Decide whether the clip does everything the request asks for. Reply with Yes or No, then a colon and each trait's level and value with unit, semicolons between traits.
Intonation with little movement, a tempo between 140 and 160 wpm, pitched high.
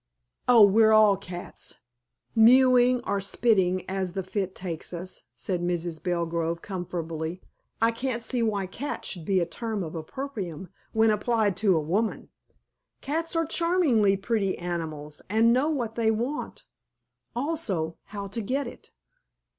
No: average, 4.9 semitones; average, 145 wpm; high, 200 Hz